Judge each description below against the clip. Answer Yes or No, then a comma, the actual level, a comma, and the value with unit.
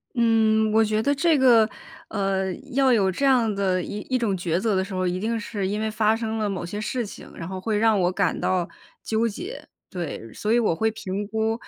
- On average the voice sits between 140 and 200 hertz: No, high, 215 Hz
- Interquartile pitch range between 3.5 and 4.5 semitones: No, average, 3.0 semitones